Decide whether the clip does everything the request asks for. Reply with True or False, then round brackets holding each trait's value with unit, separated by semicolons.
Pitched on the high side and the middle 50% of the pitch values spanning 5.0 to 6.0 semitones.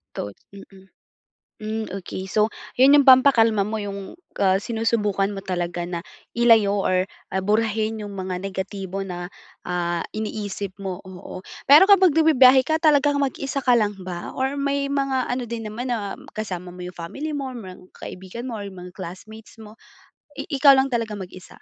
True (215 Hz; 5.3 semitones)